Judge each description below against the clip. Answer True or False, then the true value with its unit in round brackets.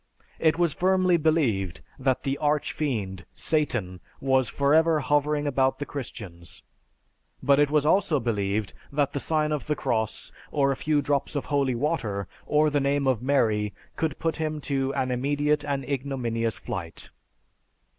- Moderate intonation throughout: True (4.1 semitones)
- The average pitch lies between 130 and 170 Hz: True (140 Hz)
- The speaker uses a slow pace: False (155 wpm)